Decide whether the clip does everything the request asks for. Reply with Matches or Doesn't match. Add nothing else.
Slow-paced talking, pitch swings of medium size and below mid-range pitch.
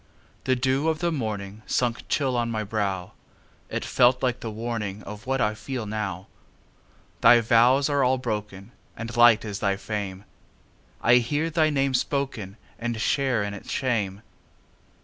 Matches